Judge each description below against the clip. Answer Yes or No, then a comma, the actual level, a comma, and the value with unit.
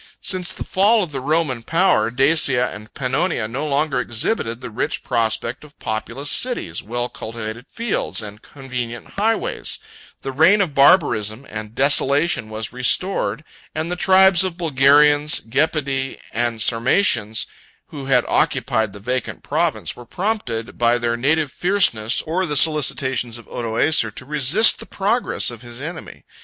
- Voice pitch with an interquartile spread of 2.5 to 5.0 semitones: No, wide, 5.6 semitones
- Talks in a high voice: No, low, 135 Hz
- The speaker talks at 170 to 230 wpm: No, average, 150 wpm